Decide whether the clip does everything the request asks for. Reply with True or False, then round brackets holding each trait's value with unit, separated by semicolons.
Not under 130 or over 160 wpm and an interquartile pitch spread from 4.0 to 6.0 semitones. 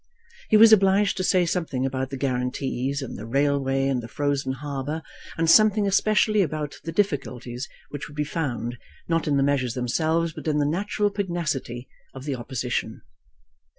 False (170 wpm; 4.6 semitones)